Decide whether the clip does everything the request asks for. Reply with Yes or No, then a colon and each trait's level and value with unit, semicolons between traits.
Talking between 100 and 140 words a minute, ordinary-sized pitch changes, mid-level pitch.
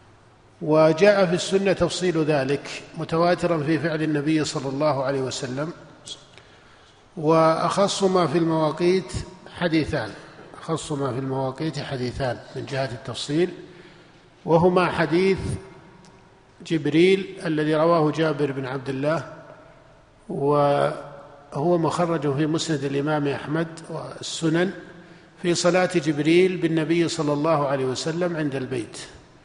Yes: average, 105 wpm; average, 3.5 semitones; medium, 155 Hz